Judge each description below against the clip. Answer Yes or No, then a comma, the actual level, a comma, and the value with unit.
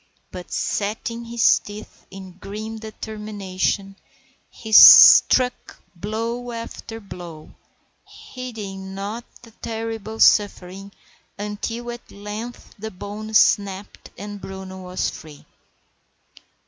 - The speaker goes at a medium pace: No, slow, 95 wpm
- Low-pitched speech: No, high, 210 Hz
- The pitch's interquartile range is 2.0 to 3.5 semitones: Yes, narrow, 2.6 semitones